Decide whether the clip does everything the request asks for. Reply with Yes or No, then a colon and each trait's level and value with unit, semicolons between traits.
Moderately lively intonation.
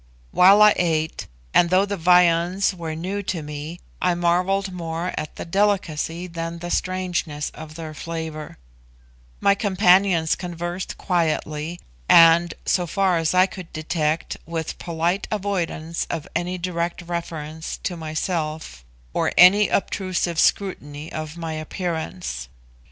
No: narrow, 2.3 semitones